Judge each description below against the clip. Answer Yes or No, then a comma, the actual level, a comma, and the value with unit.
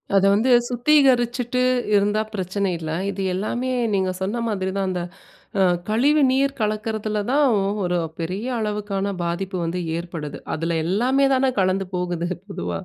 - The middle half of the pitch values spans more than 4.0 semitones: Yes, average, 4.7 semitones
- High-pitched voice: Yes, high, 205 Hz